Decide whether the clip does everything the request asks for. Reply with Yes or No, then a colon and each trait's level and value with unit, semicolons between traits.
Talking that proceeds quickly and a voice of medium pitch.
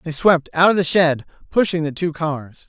Yes: fast, 225 wpm; medium, 160 Hz